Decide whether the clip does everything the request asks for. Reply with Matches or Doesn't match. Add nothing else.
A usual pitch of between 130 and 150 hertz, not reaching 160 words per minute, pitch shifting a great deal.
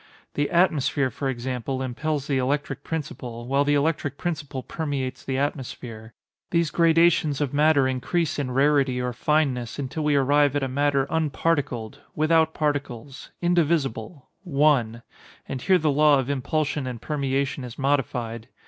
Doesn't match